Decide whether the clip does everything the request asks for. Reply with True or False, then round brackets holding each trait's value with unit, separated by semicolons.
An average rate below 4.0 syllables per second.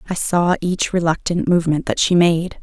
False (5.1 syllables/s)